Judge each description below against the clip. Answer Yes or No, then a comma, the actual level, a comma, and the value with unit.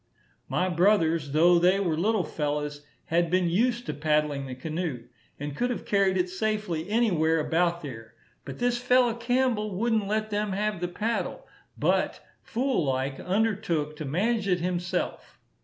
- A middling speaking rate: Yes, average, 155 wpm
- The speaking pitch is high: No, medium, 180 Hz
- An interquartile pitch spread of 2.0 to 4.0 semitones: No, wide, 5.4 semitones